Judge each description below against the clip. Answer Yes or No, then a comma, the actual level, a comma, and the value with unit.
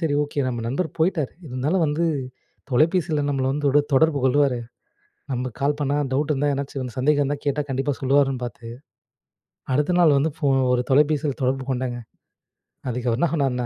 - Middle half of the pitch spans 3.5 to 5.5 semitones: No, narrow, 2.4 semitones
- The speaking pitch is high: No, medium, 140 Hz